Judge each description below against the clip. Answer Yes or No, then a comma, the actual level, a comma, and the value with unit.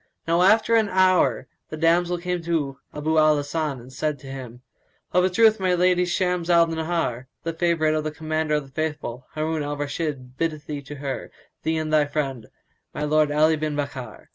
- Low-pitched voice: No, medium, 155 Hz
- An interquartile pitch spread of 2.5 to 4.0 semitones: Yes, average, 2.8 semitones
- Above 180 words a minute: Yes, average, 195 wpm